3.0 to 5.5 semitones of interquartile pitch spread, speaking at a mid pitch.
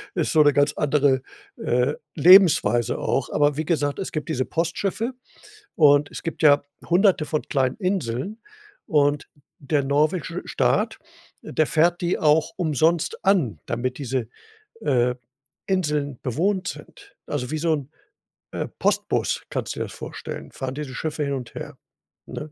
Yes: average, 3.7 semitones; medium, 150 Hz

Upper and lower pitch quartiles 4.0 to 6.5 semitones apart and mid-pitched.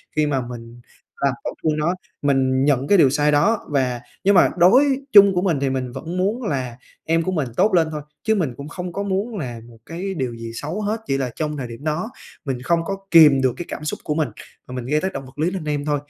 Yes: wide, 5.6 semitones; medium, 150 Hz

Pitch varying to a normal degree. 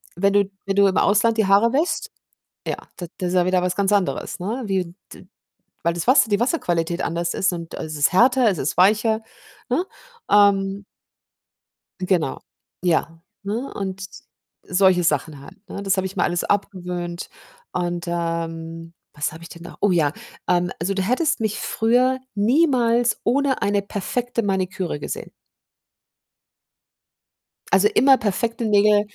Yes: average, 3.9 semitones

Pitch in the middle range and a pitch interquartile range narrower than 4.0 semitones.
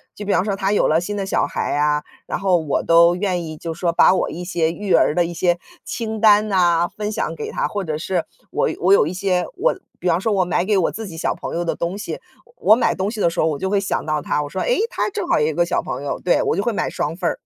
Yes: medium, 180 Hz; average, 3.3 semitones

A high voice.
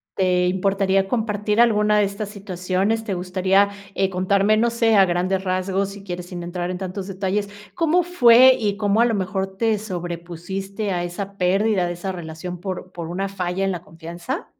Yes: high, 195 Hz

